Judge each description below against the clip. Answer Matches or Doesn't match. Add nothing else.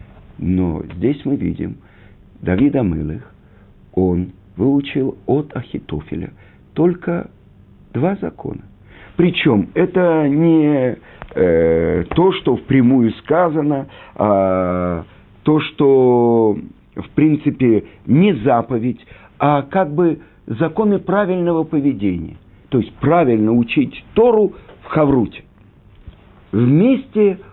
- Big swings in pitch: Matches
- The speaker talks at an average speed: Doesn't match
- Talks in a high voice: Doesn't match